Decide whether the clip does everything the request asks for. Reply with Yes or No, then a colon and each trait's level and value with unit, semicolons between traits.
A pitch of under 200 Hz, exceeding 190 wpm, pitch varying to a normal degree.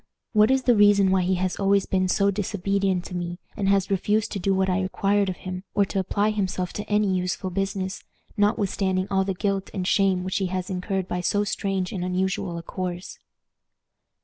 No: high, 190 Hz; average, 200 wpm; narrow, 1.5 semitones